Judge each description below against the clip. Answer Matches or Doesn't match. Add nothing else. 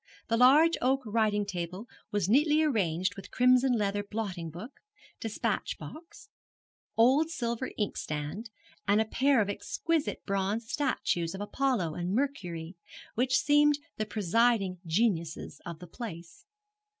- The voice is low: Doesn't match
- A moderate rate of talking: Doesn't match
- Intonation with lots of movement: Matches